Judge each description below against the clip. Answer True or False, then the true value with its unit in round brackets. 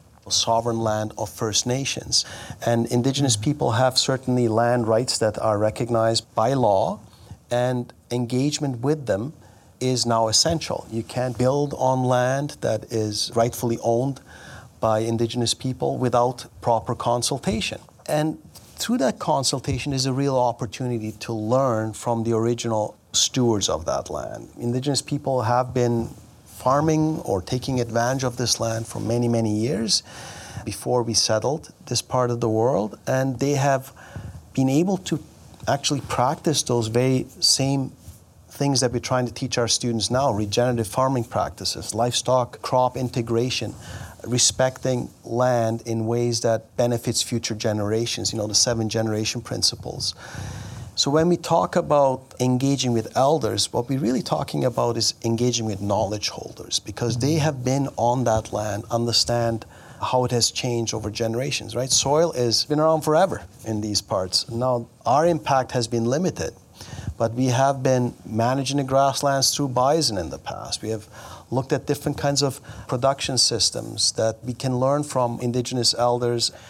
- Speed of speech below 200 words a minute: True (150 wpm)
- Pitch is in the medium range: False (120 Hz)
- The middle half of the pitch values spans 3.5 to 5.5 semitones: False (2.7 semitones)